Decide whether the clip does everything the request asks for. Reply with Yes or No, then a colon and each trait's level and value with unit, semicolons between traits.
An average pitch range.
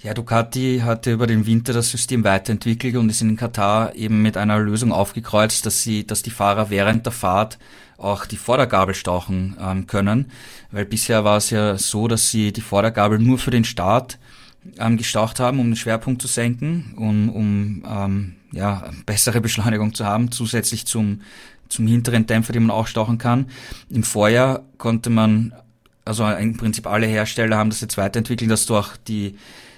No: narrow, 1.9 semitones